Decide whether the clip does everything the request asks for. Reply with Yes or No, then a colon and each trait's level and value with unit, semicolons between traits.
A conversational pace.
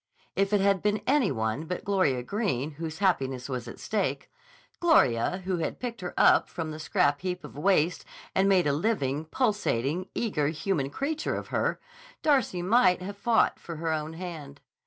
Yes: average, 180 wpm